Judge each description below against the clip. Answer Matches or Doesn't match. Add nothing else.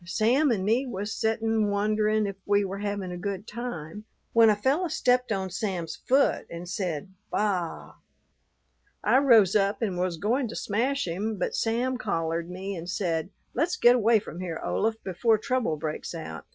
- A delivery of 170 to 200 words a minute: Matches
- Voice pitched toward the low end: Doesn't match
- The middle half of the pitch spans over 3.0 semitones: Matches